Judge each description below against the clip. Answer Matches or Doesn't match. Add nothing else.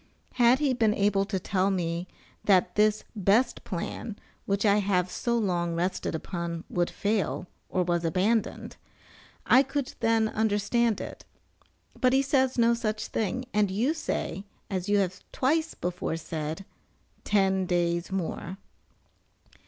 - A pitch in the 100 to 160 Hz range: Doesn't match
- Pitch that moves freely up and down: Doesn't match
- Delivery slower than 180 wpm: Matches